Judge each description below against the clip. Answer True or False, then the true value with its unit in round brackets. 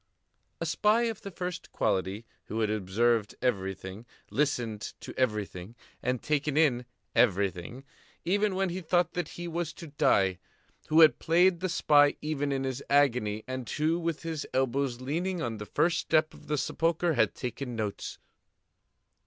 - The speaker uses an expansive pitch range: True (6.8 semitones)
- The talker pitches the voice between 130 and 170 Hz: True (140 Hz)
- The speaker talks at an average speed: True (160 wpm)